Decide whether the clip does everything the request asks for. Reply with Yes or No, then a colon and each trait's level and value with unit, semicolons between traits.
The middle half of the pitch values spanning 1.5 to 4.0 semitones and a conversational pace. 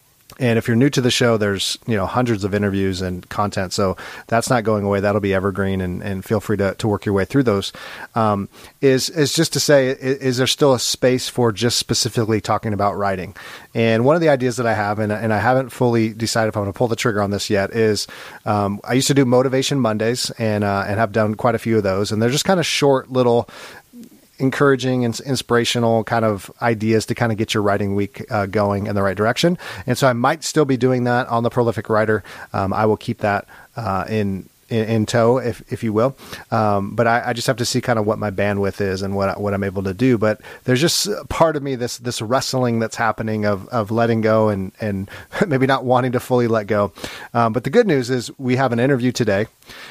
No: average, 3.5 semitones; fast, 240 wpm